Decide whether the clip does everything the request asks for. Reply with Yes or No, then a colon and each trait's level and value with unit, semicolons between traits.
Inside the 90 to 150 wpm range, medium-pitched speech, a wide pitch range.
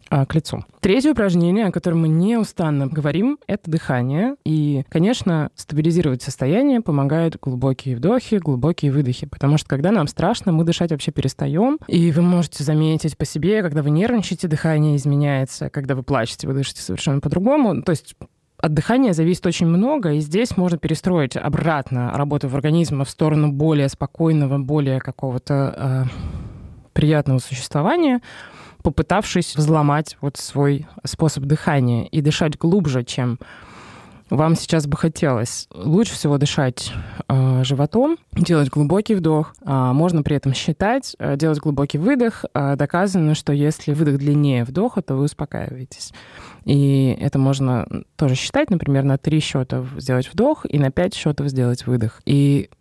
No: average, 145 wpm; medium, 150 Hz; average, 3.8 semitones